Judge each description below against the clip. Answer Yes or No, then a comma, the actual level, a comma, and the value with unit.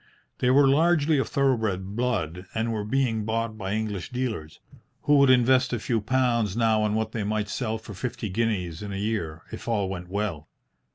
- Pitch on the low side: Yes, low, 110 Hz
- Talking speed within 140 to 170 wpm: No, average, 190 wpm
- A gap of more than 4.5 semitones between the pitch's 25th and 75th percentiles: No, average, 3.7 semitones